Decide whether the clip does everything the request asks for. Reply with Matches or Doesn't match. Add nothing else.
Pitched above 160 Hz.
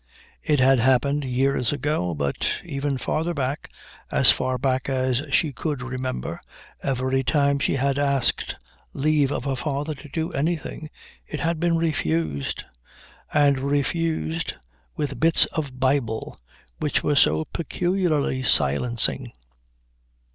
Doesn't match